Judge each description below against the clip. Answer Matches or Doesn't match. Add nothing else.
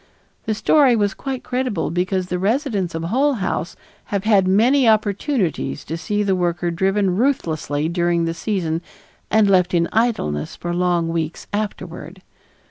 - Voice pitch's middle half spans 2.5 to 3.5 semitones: Doesn't match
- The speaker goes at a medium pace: Matches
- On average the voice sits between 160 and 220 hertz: Matches